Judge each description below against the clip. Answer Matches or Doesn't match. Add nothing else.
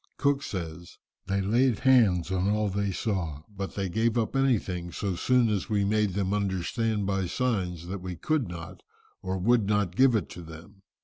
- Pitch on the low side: Matches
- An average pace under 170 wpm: Doesn't match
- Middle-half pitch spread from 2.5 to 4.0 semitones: Matches